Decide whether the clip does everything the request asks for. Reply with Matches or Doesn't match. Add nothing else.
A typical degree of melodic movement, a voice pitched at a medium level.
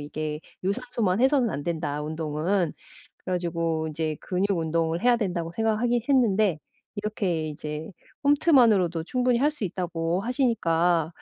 Doesn't match